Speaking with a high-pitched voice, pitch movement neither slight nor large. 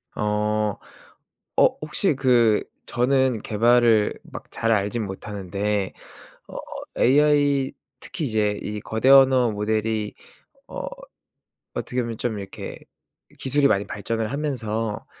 No: low, 115 Hz; average, 3.8 semitones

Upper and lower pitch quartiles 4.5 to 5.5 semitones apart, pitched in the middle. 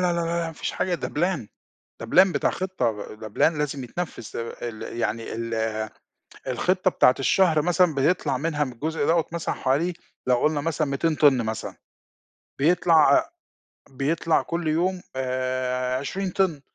Yes: average, 5.2 semitones; medium, 150 Hz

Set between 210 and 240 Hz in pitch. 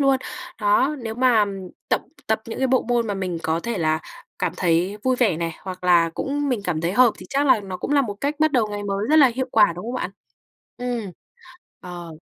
Yes: high, 215 Hz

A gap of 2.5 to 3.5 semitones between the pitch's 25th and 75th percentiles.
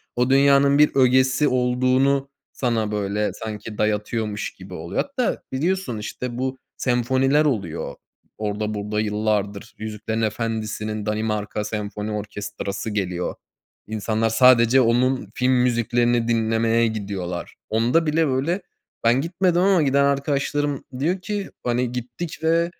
No: average, 4.1 semitones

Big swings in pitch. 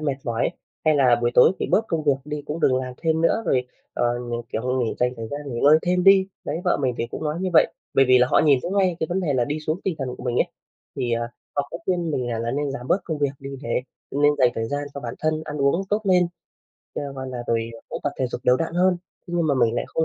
No: average, 4.8 semitones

